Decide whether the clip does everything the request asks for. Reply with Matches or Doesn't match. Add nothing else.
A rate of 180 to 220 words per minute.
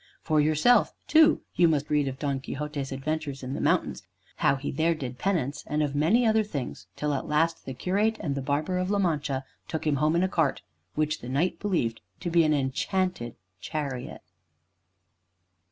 Matches